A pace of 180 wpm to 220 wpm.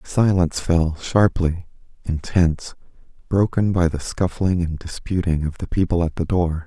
No: average, 145 wpm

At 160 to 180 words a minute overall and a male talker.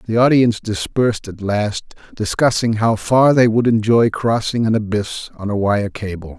Yes: average, 170 wpm; male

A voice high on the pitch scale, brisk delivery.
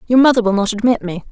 Yes: high, 220 Hz; fast, 275 wpm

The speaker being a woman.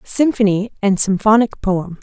Yes: female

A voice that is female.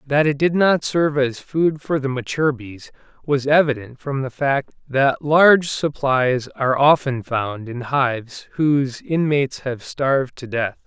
No: male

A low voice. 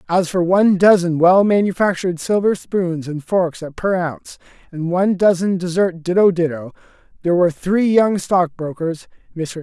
No: medium, 180 Hz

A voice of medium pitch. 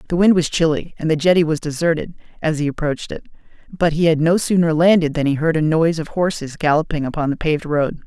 Yes: medium, 160 Hz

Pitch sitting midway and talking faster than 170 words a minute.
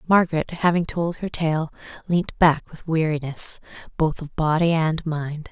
No: medium, 160 Hz; average, 150 wpm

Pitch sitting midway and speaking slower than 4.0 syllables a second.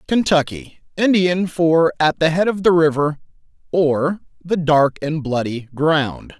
Yes: medium, 160 Hz; 3.8 syllables/s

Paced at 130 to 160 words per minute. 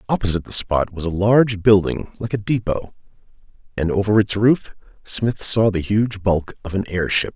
No: average, 180 wpm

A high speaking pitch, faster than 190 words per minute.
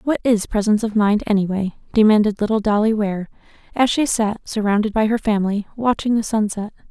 No: high, 215 Hz; average, 180 wpm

